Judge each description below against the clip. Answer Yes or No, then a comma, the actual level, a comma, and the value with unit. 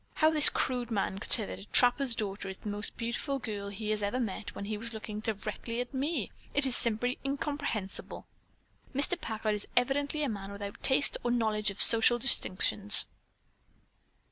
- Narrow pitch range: No, average, 4.1 semitones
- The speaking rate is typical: Yes, average, 175 wpm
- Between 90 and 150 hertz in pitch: No, high, 225 Hz